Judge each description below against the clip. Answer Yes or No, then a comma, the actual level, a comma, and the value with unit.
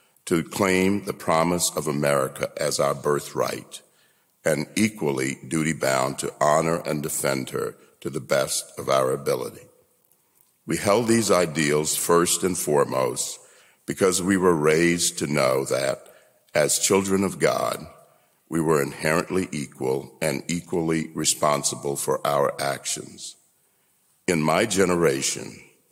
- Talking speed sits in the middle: No, slow, 125 wpm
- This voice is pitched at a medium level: No, very low, 80 Hz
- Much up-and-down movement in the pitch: No, average, 3.9 semitones